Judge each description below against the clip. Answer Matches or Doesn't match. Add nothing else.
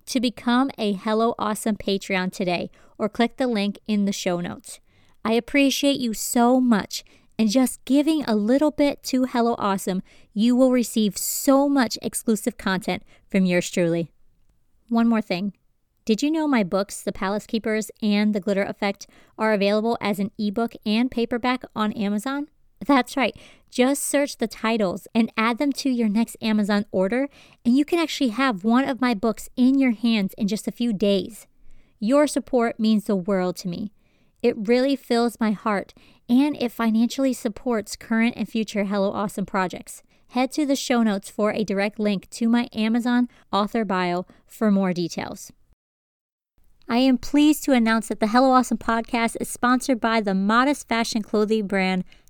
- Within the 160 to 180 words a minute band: Matches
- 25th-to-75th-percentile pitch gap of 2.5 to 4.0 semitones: Matches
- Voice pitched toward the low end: Doesn't match